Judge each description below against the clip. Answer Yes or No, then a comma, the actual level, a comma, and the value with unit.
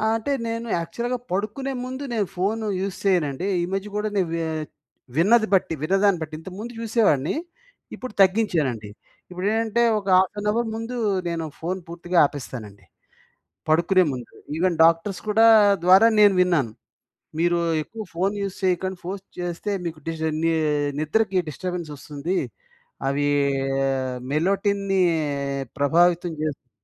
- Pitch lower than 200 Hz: Yes, medium, 185 Hz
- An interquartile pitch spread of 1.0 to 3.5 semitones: No, average, 4.2 semitones